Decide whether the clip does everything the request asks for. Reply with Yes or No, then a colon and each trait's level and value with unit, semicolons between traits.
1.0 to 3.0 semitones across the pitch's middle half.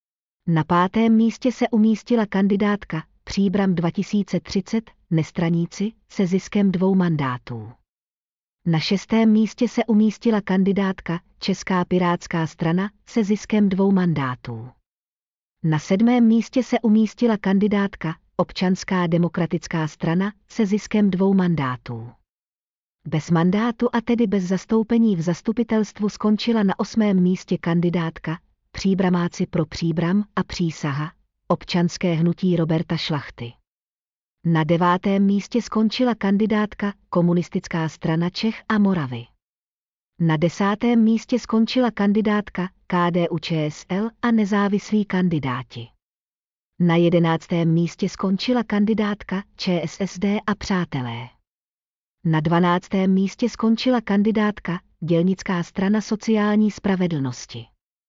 No: average, 4.4 semitones